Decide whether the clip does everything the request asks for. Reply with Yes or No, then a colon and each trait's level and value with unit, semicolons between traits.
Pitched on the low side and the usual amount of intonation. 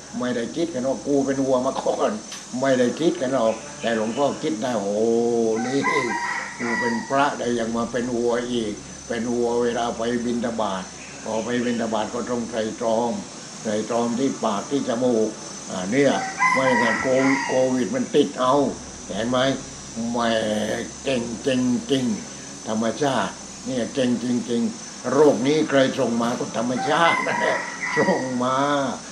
Yes: low, 125 Hz; average, 3.3 semitones